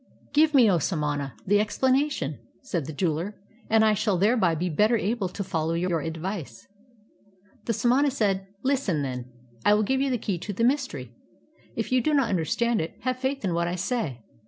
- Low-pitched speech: No, high, 205 Hz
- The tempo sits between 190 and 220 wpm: Yes, average, 195 wpm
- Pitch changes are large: Yes, wide, 6.9 semitones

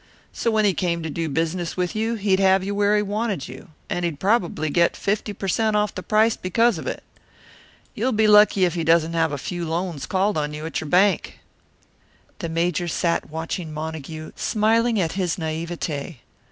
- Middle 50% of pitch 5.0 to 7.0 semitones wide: No, average, 4.3 semitones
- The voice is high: No, medium, 180 Hz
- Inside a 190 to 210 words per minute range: Yes, average, 195 wpm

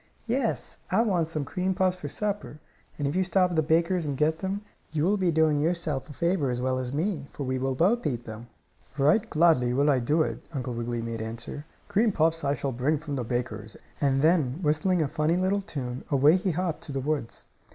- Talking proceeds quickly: Yes, fast, 225 wpm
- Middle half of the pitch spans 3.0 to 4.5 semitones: No, average, 5.2 semitones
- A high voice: No, medium, 150 Hz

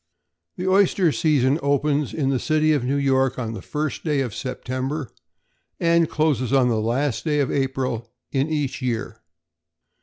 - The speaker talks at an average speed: Yes, average, 160 wpm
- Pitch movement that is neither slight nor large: Yes, average, 3.0 semitones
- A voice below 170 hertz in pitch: Yes, low, 135 Hz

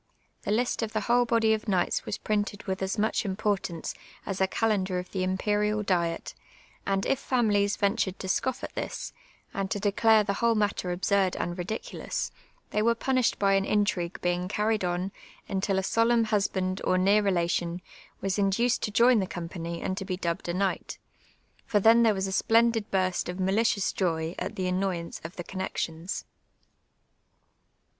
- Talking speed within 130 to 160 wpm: No, average, 175 wpm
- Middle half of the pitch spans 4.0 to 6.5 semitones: No, average, 2.8 semitones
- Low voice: No, high, 195 Hz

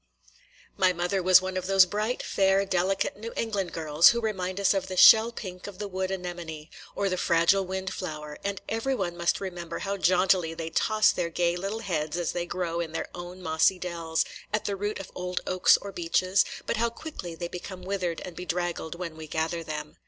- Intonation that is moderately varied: No, narrow, 2.3 semitones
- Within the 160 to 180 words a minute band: No, fast, 205 wpm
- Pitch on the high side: No, medium, 180 Hz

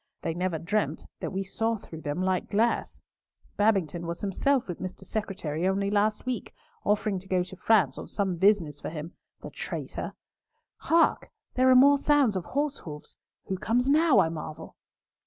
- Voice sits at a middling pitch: No, high, 195 Hz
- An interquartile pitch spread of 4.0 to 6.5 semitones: Yes, average, 4.7 semitones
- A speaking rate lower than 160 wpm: No, average, 165 wpm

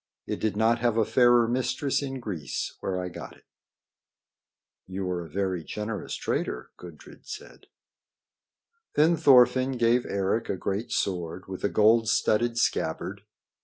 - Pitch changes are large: No, average, 4.5 semitones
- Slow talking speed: No, average, 145 wpm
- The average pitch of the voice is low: Yes, low, 110 Hz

